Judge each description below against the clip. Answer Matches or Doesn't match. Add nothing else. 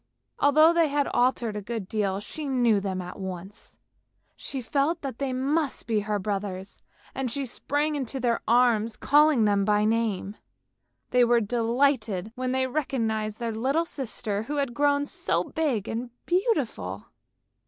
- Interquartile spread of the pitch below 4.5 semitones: Doesn't match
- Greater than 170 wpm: Doesn't match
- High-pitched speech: Matches